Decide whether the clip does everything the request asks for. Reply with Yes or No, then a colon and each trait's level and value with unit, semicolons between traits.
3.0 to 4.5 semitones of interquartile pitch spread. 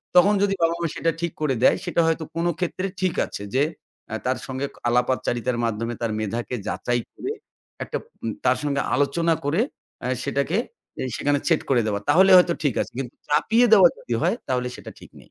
No: wide, 5.6 semitones